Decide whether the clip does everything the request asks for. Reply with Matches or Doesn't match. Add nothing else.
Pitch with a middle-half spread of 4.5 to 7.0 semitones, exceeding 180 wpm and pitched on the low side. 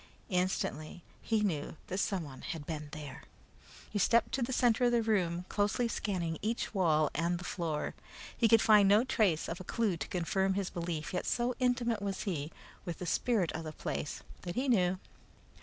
Doesn't match